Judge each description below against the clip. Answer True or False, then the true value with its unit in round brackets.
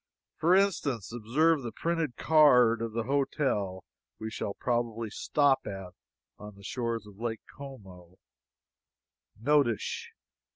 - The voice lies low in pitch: True (120 Hz)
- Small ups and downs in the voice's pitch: False (5.1 semitones)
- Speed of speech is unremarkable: False (120 wpm)